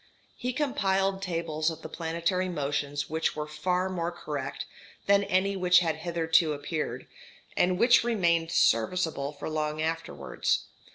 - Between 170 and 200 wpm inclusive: No, slow, 135 wpm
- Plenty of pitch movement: No, average, 3.3 semitones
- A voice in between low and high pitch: Yes, medium, 165 Hz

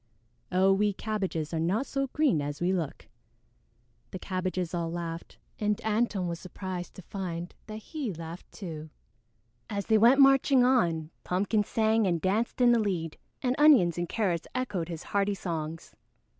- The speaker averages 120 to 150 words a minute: No, average, 160 wpm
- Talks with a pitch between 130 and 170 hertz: No, high, 190 Hz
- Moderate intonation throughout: Yes, average, 4.5 semitones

